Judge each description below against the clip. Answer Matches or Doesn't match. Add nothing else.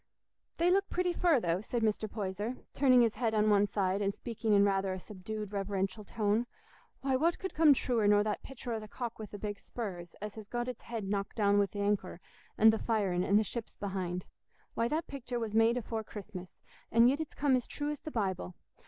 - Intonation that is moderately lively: Matches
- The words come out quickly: Matches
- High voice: Matches